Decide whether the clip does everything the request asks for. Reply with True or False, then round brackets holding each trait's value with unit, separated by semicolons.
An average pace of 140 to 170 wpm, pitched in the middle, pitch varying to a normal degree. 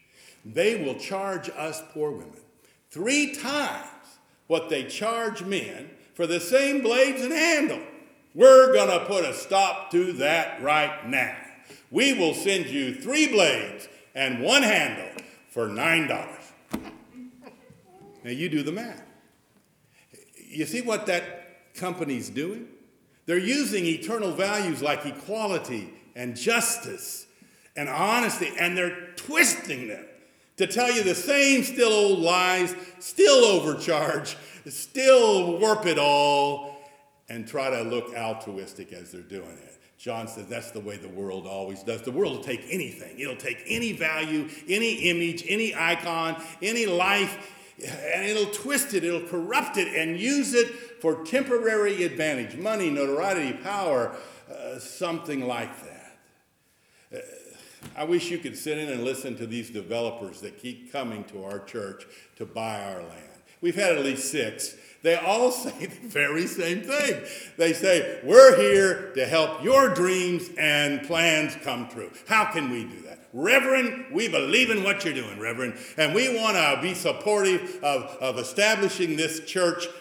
False (150 wpm; 180 Hz; 7.6 semitones)